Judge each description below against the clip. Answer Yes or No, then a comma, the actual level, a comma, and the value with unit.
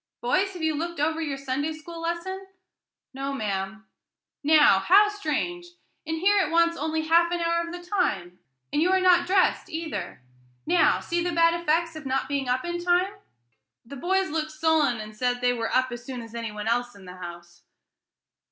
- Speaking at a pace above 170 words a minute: Yes, average, 195 wpm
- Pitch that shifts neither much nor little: No, wide, 5.8 semitones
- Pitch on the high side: Yes, very high, 315 Hz